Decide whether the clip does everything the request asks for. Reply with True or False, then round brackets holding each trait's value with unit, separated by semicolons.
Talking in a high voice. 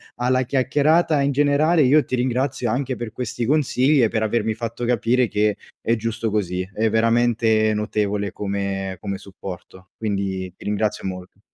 False (115 Hz)